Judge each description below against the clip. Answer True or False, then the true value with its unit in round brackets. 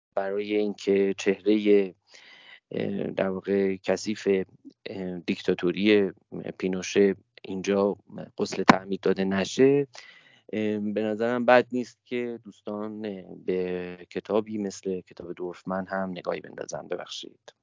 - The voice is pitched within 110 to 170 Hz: False (100 Hz)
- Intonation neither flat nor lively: False (2.1 semitones)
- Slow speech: True (95 wpm)